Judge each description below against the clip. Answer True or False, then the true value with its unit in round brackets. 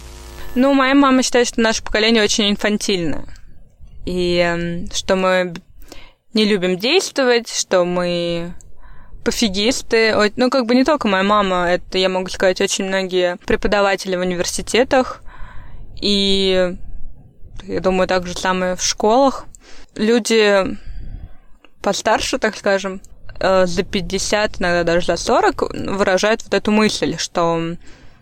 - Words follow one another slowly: False (120 wpm)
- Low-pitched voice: False (195 Hz)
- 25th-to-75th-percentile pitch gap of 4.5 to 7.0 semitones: False (3.6 semitones)